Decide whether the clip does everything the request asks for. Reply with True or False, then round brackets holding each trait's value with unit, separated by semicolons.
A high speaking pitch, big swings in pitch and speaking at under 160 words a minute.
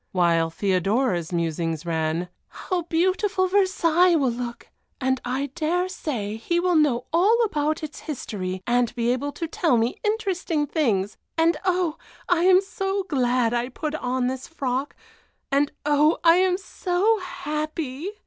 True (295 Hz; 6.8 semitones; 150 wpm)